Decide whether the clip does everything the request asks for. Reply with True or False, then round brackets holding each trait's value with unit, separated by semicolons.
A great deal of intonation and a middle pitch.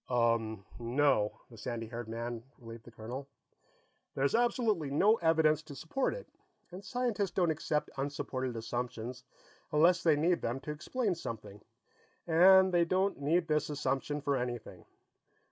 True (6.4 semitones; 145 Hz)